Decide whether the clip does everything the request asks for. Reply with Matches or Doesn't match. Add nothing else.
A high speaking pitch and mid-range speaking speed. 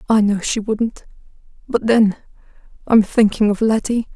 Matches